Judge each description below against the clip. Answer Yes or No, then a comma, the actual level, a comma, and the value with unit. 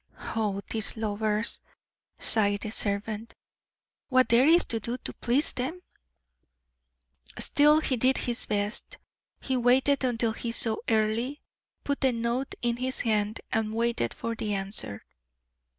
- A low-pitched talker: No, high, 230 Hz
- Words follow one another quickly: No, slow, 135 wpm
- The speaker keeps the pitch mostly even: No, average, 3.1 semitones